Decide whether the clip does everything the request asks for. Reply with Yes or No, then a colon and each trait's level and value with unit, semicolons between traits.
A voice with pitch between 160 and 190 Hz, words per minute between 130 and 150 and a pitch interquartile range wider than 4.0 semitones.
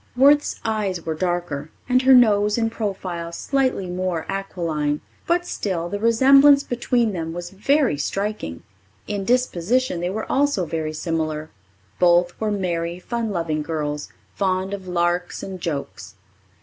Yes: medium, 185 Hz; average, 140 wpm; average, 5.2 semitones